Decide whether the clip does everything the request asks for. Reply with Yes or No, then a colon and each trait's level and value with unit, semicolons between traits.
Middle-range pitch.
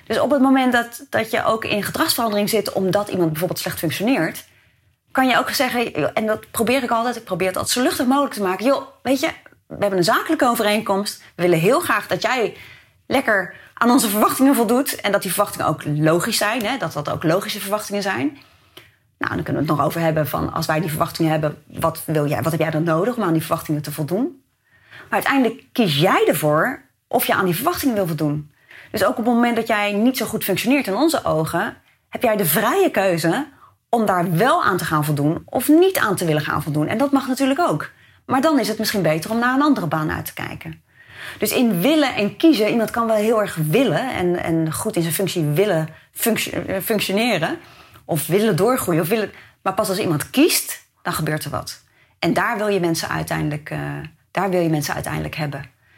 No: high, 200 Hz